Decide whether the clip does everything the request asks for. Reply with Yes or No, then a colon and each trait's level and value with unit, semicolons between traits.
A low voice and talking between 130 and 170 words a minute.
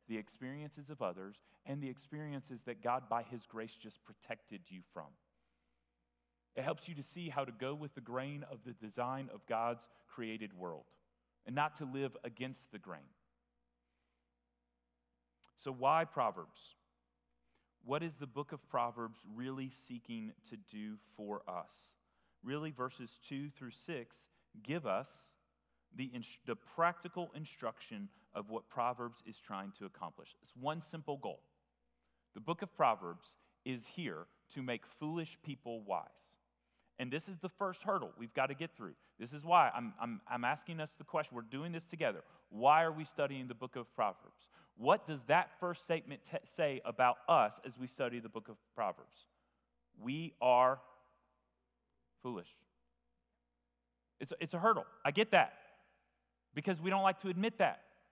Yes: low, 125 Hz; average, 160 wpm